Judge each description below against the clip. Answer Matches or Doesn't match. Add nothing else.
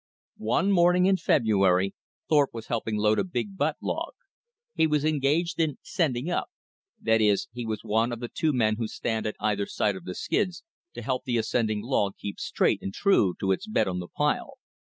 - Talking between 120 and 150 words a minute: Doesn't match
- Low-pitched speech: Matches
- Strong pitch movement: Matches